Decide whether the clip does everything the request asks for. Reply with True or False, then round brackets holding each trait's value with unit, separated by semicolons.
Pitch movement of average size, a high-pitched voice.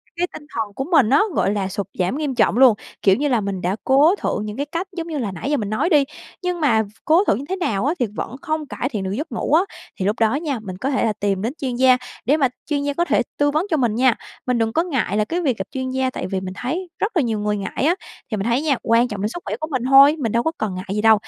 False (5.8 semitones; 255 Hz)